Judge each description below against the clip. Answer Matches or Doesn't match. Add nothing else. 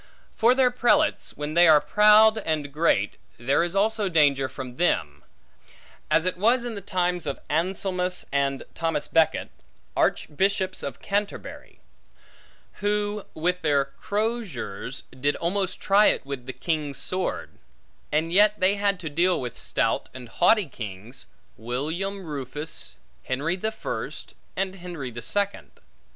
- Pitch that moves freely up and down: Matches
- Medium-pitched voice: Matches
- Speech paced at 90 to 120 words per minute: Doesn't match